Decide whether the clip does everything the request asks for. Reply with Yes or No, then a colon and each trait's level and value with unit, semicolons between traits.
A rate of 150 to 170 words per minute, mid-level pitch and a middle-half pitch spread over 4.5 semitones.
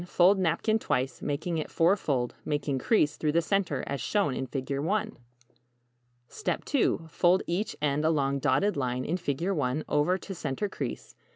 Yes: average, 160 wpm; medium, 155 Hz; average, 5.3 semitones